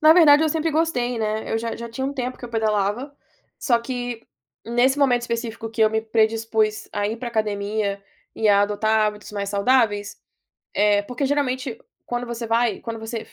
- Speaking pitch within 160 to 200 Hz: No, high, 230 Hz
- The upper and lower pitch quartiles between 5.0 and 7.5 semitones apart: No, average, 2.7 semitones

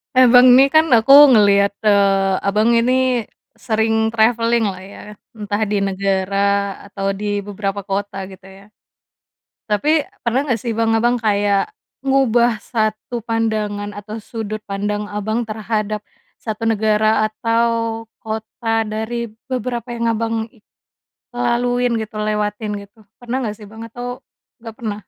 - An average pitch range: No, narrow, 2.3 semitones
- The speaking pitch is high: Yes, high, 220 Hz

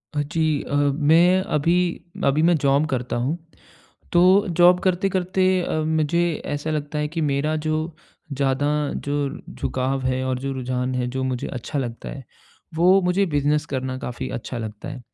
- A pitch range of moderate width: Yes, average, 4.2 semitones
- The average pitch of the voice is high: No, medium, 145 Hz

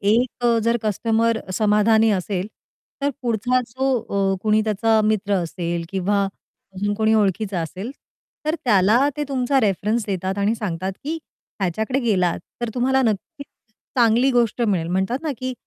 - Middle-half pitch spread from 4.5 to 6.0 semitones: No, average, 3.6 semitones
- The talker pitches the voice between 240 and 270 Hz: No, high, 220 Hz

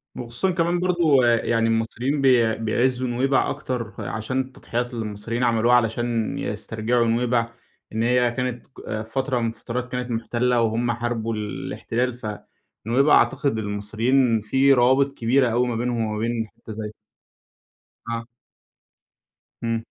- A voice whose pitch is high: No, low, 120 Hz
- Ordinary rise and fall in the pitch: No, narrow, 1.9 semitones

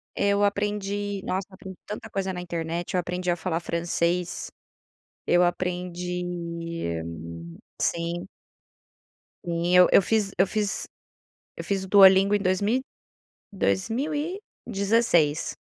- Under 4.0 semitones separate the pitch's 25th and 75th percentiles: Yes, average, 2.7 semitones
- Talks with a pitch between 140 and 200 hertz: Yes, medium, 185 Hz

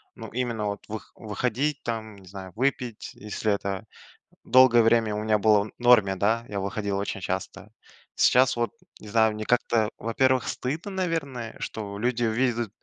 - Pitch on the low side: Yes, low, 110 Hz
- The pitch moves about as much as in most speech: Yes, average, 3.1 semitones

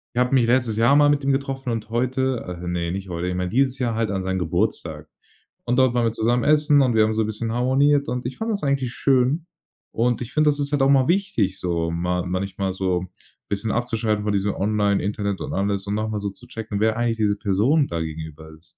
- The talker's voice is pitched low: Yes, low, 110 Hz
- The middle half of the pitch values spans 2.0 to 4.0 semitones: No, average, 5.1 semitones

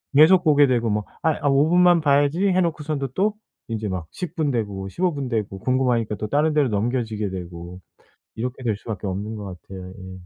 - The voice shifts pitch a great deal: Yes, wide, 6.9 semitones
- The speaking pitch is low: Yes, low, 125 Hz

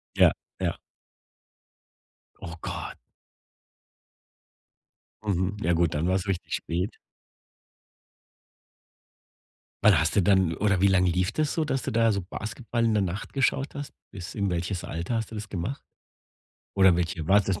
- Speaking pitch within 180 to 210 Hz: No, very low, 95 Hz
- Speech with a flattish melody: No, average, 3.5 semitones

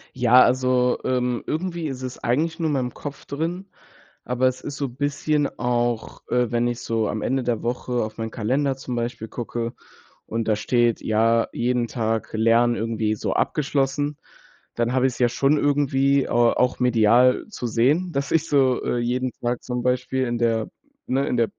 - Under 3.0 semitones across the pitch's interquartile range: Yes, narrow, 2.6 semitones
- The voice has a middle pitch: No, low, 125 Hz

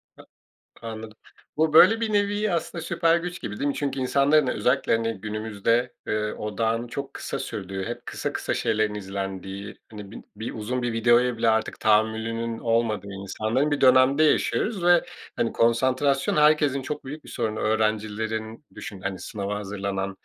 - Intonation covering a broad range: No, average, 4.7 semitones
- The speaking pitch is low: Yes, low, 115 Hz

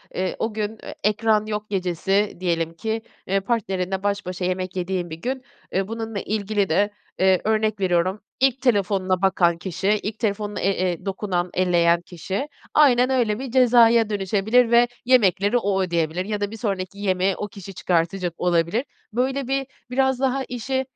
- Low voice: No, high, 200 Hz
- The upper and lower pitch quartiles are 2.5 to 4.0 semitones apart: Yes, average, 3.6 semitones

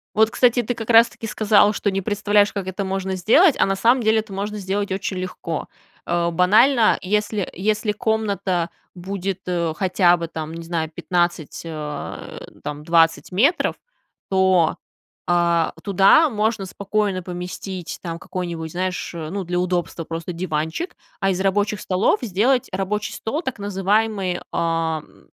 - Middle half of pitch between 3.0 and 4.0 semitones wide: Yes, average, 3.4 semitones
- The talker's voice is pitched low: No, high, 190 Hz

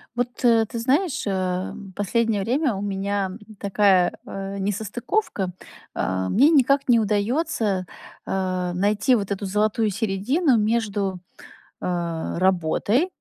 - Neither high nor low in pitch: No, high, 205 Hz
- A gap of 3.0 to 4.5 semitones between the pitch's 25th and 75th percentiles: Yes, average, 3.7 semitones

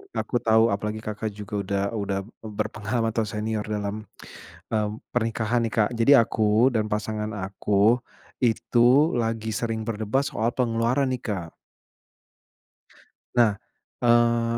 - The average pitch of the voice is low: Yes, low, 110 Hz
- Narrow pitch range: Yes, narrow, 1.9 semitones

